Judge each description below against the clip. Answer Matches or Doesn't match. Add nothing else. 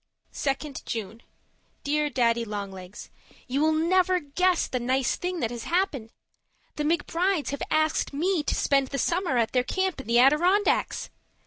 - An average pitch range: Doesn't match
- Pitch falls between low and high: Doesn't match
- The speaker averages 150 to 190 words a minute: Matches